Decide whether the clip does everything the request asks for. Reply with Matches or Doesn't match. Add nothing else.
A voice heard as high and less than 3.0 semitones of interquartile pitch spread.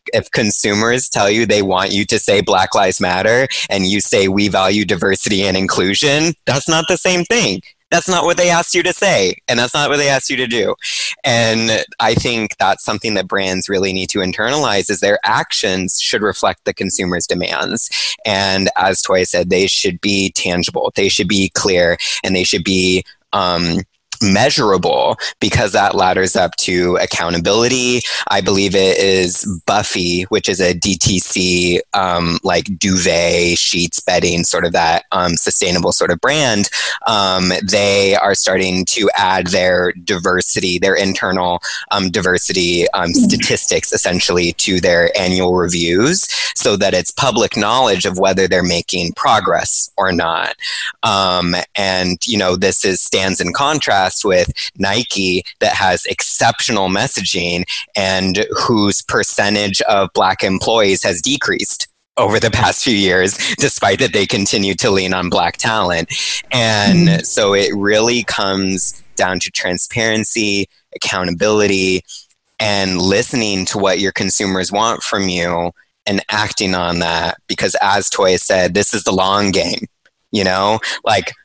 Doesn't match